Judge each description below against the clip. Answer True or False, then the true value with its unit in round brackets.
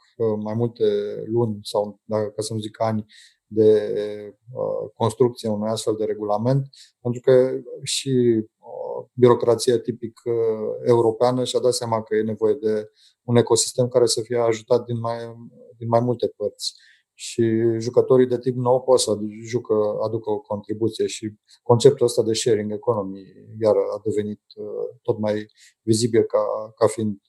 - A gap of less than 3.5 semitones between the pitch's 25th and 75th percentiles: True (2.5 semitones)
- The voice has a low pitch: True (115 Hz)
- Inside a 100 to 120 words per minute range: False (145 wpm)